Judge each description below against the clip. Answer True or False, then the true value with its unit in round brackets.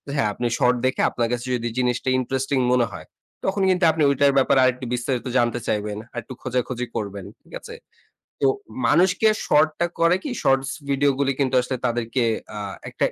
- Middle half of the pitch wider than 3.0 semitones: False (2.7 semitones)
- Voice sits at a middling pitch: False (130 Hz)